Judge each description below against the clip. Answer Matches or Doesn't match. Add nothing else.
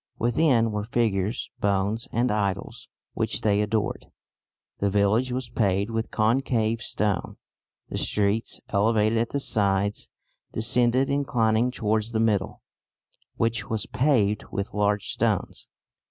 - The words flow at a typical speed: Doesn't match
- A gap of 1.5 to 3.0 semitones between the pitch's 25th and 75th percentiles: Matches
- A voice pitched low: Matches